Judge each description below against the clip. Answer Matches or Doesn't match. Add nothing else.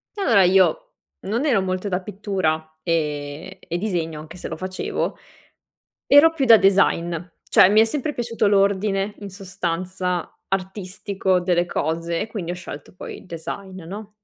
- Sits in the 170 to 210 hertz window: Matches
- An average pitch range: Matches